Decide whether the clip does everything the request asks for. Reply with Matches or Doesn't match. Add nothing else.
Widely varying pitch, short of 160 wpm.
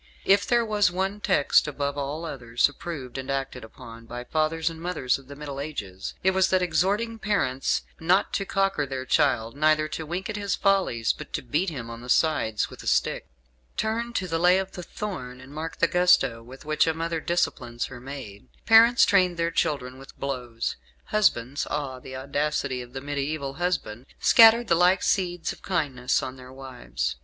Doesn't match